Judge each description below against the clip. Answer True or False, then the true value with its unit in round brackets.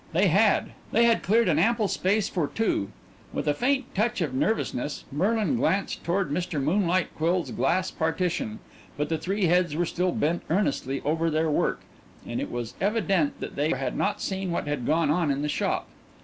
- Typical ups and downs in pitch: True (4.8 semitones)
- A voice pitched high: False (175 Hz)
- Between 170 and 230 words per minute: True (190 wpm)